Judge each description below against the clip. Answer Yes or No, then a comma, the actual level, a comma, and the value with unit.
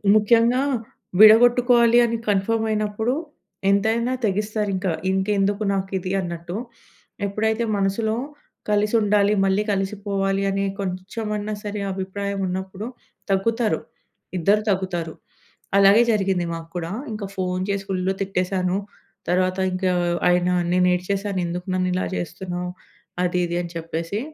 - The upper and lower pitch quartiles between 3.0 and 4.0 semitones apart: No, narrow, 2.4 semitones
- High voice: Yes, high, 195 Hz